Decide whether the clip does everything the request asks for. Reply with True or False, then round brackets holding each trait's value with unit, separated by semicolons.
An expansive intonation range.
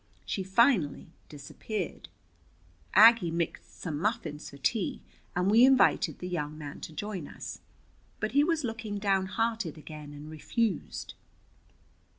True (6.5 semitones)